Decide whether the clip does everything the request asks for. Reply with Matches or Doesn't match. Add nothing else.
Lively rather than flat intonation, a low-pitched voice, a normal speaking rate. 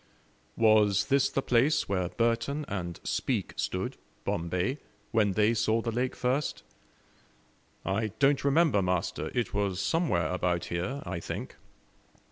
Doesn't match